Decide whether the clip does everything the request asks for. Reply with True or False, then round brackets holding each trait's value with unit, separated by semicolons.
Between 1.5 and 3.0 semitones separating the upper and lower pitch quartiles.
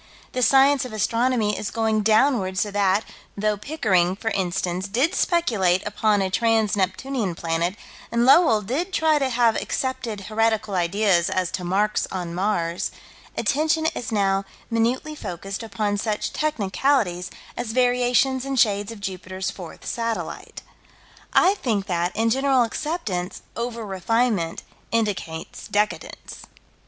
False (4.6 semitones)